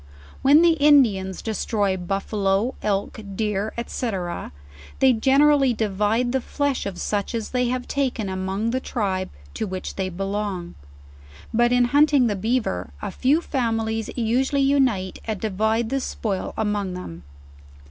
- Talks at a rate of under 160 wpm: Yes, average, 140 wpm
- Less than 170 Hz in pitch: No, high, 220 Hz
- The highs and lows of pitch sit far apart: No, average, 4.6 semitones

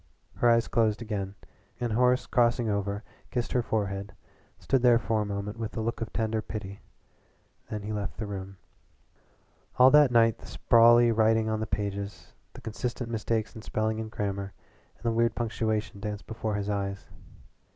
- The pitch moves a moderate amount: No, narrow, 2.3 semitones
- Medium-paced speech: Yes, average, 170 wpm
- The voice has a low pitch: Yes, low, 110 Hz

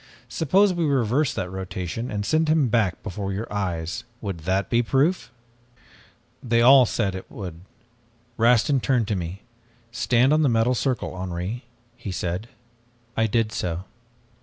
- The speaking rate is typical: Yes, average, 155 wpm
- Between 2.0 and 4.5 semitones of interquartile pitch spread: No, wide, 5.4 semitones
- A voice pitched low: Yes, low, 115 Hz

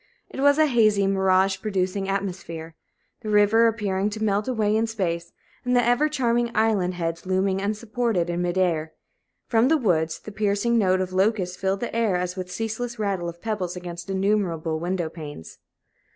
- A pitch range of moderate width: Yes, average, 3.7 semitones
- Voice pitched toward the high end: Yes, high, 195 Hz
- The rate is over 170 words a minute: Yes, average, 180 wpm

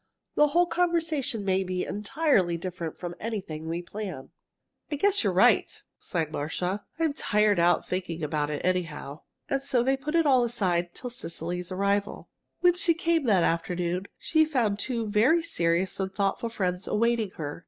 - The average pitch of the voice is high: Yes, high, 200 Hz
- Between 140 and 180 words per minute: Yes, average, 165 wpm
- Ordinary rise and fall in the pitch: No, wide, 7.4 semitones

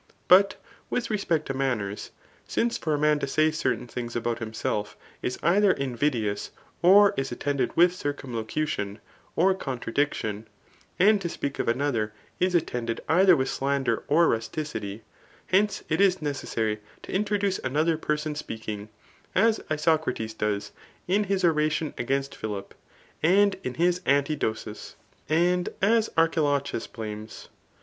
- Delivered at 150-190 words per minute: No, average, 140 wpm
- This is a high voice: No, medium, 145 Hz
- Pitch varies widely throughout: Yes, wide, 7.2 semitones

